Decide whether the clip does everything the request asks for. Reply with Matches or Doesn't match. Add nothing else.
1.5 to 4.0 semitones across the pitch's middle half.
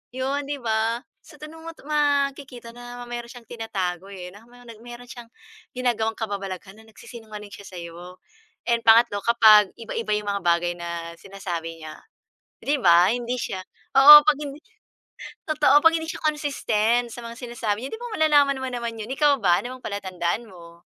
Doesn't match